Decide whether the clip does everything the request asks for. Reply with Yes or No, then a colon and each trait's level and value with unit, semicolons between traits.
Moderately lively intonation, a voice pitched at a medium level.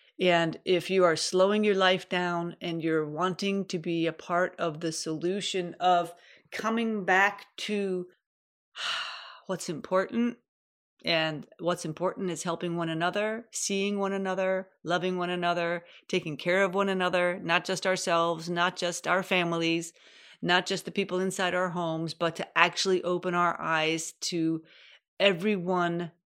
No: narrow, 1.9 semitones; medium, 180 Hz